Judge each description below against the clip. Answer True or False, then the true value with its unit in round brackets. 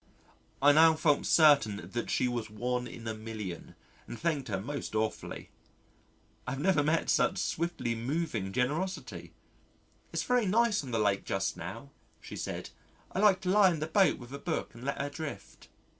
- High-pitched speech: False (140 Hz)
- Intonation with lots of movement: True (6.5 semitones)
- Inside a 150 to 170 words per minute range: False (180 wpm)